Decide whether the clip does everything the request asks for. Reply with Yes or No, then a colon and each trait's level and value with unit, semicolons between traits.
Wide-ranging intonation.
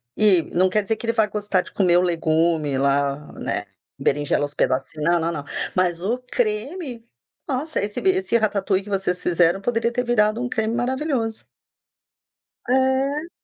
Yes: wide, 5.9 semitones